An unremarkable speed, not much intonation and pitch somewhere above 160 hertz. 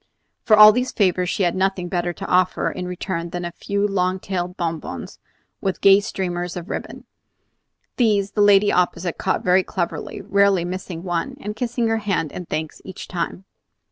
Yes: average, 175 wpm; narrow, 2.3 semitones; medium, 185 Hz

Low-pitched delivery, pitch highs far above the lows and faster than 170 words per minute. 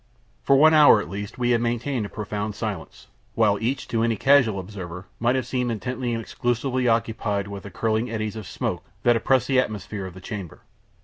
No: low, 115 Hz; average, 3.3 semitones; average, 200 wpm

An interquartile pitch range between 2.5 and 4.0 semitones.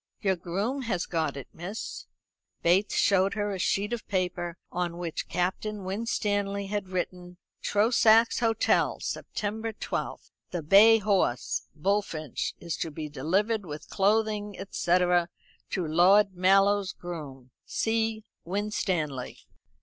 Yes: average, 3.2 semitones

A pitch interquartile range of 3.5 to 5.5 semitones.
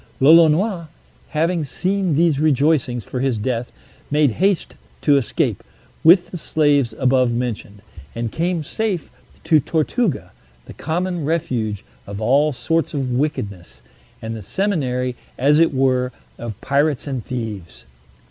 Yes: average, 5.1 semitones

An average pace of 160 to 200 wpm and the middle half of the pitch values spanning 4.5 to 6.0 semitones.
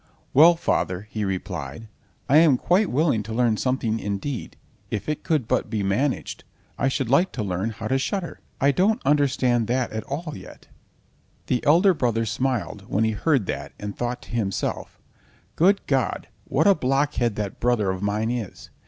Yes: average, 170 wpm; average, 5.3 semitones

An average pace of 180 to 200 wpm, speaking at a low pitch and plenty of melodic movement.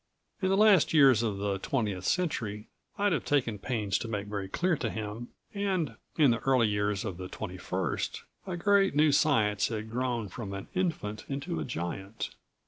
Yes: average, 185 wpm; low, 115 Hz; wide, 6.8 semitones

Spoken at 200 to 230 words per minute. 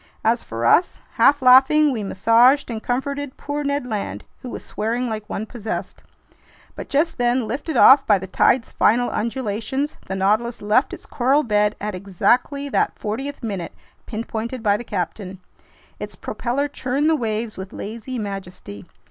No: average, 160 wpm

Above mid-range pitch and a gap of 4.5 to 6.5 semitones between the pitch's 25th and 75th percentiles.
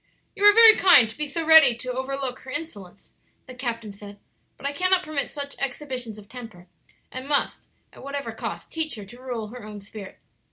Yes: very high, 255 Hz; average, 5.0 semitones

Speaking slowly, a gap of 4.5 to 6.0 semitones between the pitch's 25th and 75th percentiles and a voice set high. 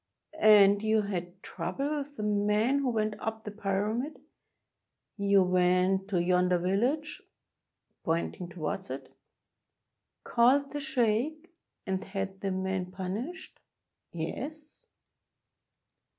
Yes: slow, 110 wpm; average, 5.1 semitones; high, 205 Hz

